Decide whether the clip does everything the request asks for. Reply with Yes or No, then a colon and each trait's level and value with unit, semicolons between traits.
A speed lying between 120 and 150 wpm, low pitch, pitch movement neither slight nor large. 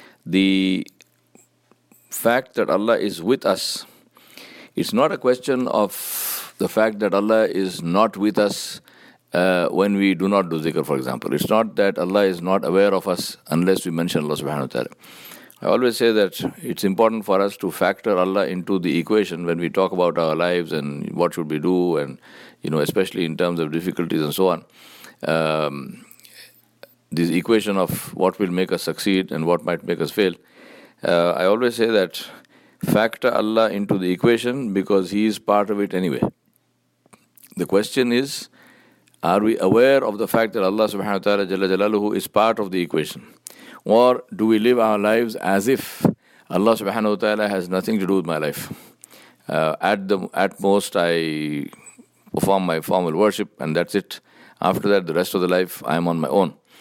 No: average, 185 wpm; very low, 95 Hz; average, 3.4 semitones